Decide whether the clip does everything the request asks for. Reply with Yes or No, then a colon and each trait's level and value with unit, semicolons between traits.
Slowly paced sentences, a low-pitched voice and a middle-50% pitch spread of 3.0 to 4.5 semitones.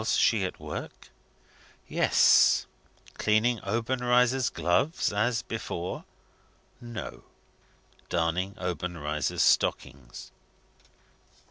No: slow, 75 wpm; low, 105 Hz; wide, 5.5 semitones